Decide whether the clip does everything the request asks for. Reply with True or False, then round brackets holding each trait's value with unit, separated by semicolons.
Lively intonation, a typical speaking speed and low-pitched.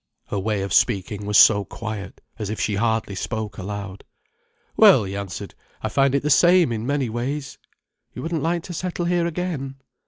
True (6.7 semitones; 185 wpm; 115 Hz)